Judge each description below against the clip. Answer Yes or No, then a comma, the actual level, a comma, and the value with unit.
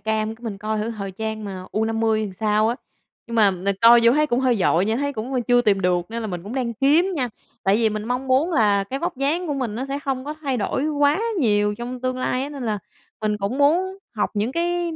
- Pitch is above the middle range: Yes, high, 235 Hz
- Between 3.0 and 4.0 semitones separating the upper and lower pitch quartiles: No, average, 4.5 semitones